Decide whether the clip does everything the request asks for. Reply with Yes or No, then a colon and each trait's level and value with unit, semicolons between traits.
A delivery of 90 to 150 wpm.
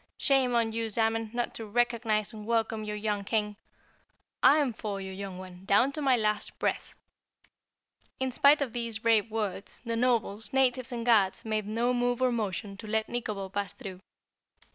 No: average, 175 wpm